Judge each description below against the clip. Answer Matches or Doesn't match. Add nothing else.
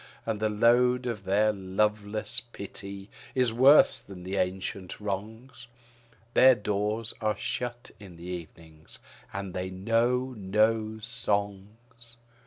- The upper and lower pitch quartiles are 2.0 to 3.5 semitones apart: Matches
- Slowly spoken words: Matches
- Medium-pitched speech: Doesn't match